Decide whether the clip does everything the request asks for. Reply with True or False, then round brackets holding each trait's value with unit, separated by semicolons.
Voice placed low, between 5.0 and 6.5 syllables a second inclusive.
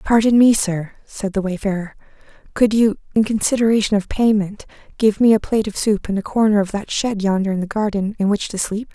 False (205 Hz; 5.8 syllables/s)